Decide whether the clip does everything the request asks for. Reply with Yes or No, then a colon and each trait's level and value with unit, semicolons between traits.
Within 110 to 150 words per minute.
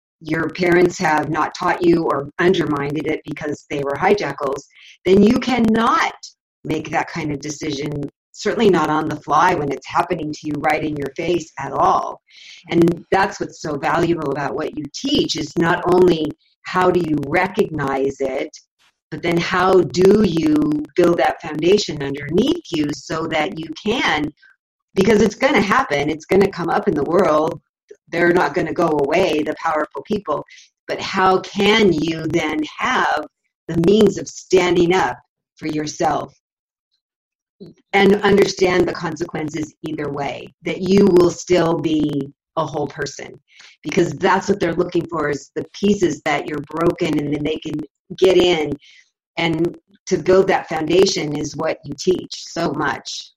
No: average, 165 wpm